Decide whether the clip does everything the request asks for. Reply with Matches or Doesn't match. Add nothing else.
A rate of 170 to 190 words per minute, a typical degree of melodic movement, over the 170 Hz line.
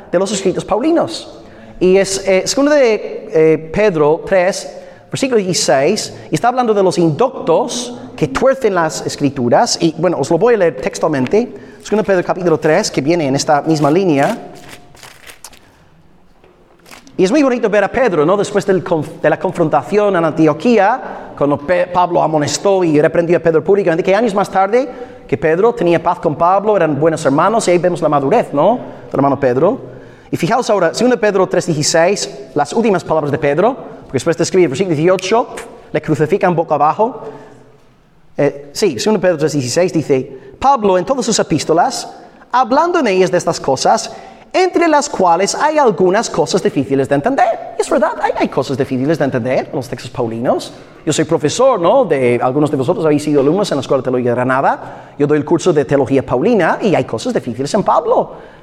Doesn't match